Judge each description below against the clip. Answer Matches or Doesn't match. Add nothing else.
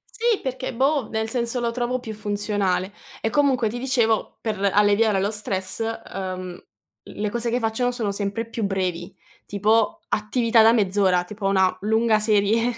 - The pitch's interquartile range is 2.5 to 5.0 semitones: Matches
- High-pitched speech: Matches